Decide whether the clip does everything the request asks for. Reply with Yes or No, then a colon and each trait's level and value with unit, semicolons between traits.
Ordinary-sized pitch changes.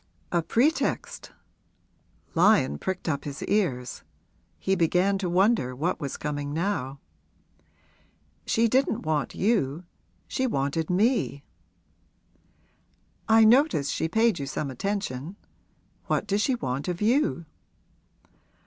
No: wide, 7.2 semitones